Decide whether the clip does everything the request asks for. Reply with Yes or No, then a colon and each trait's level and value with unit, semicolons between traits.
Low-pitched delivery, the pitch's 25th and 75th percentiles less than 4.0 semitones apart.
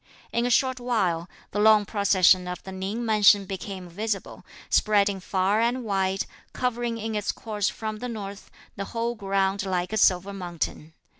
No: high, 200 Hz; average, 2.7 semitones